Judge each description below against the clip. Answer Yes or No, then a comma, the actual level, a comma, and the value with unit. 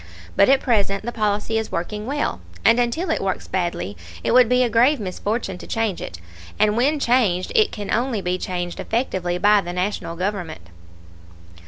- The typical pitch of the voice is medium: No, high, 210 Hz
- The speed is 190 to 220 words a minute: No, average, 180 wpm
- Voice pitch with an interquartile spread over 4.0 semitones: Yes, average, 4.8 semitones